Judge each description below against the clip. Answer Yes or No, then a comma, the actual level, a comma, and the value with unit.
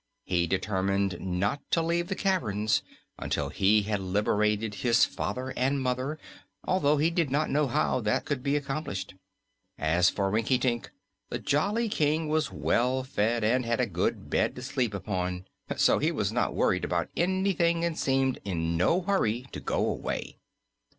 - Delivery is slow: No, average, 165 wpm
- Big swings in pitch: Yes, wide, 7.0 semitones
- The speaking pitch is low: Yes, low, 125 Hz